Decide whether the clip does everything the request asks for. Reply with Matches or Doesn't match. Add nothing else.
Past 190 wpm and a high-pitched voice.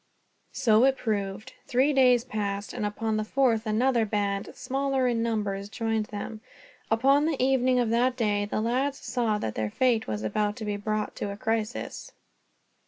Doesn't match